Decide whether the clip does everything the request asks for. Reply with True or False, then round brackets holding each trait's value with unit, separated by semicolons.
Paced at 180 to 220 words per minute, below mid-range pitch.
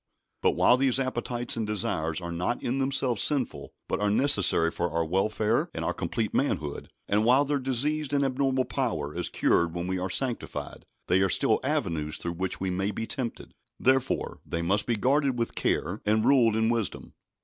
True (190 wpm; 110 Hz)